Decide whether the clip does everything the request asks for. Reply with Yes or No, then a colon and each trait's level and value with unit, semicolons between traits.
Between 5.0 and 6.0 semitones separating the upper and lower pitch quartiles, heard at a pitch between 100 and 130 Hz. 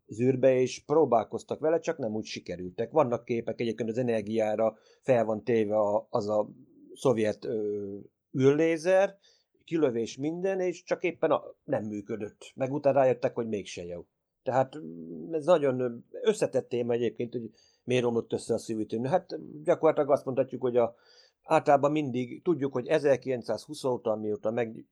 Yes: wide, 5.4 semitones; low, 125 Hz